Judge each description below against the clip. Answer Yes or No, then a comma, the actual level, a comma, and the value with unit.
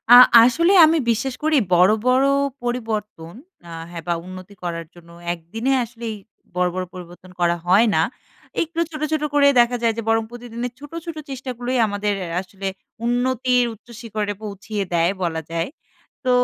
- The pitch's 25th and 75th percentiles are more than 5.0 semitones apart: Yes, wide, 5.5 semitones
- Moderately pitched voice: No, high, 225 Hz